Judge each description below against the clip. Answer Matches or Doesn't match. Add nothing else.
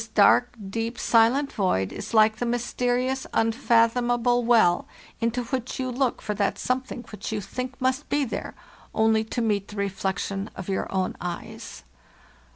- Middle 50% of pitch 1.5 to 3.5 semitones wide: Matches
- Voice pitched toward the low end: Doesn't match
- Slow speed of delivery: Doesn't match